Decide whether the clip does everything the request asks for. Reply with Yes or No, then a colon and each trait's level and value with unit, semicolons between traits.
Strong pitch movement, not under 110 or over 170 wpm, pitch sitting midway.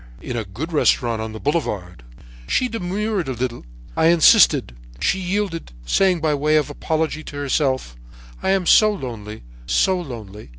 Yes: wide, 8.0 semitones; average, 155 wpm; medium, 150 Hz